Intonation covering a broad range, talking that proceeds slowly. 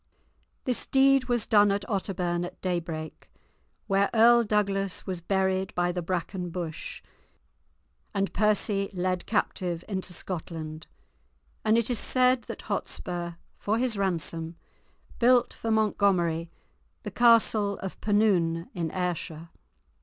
No: average, 3.7 semitones; slow, 125 wpm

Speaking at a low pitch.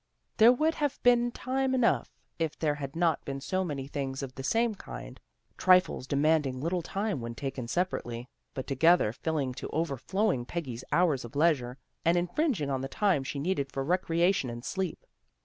No: medium, 155 Hz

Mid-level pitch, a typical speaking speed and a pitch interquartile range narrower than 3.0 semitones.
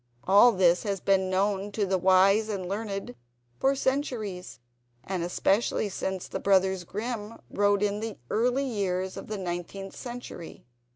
No: high, 200 Hz; average, 150 wpm; narrow, 2.5 semitones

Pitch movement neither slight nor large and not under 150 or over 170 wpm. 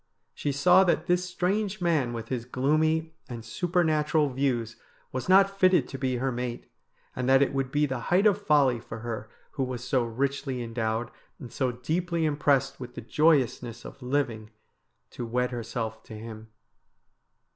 Yes: average, 4.8 semitones; average, 165 wpm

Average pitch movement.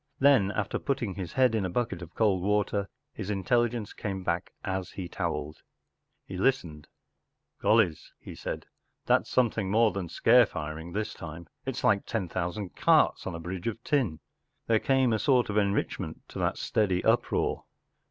Yes: average, 4.4 semitones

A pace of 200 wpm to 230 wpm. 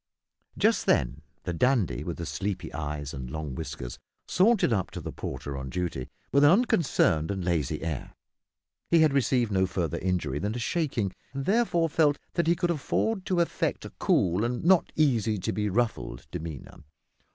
No: average, 175 wpm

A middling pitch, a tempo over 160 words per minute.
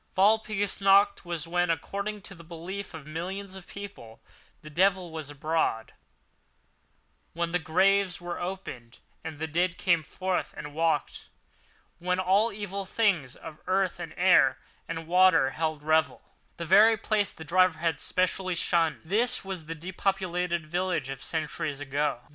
No: medium, 175 Hz; average, 145 wpm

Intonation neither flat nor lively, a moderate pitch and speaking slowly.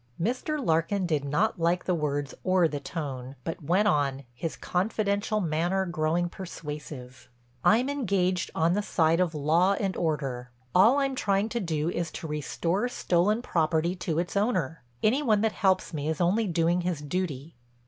No: average, 4.3 semitones; medium, 175 Hz; average, 170 wpm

